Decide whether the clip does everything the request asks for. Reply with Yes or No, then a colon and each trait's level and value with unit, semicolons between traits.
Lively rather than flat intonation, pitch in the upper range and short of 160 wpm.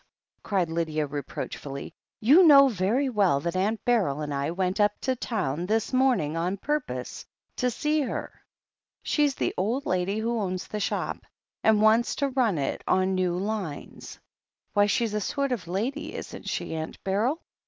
No: wide, 6.0 semitones; high, 205 Hz; average, 165 wpm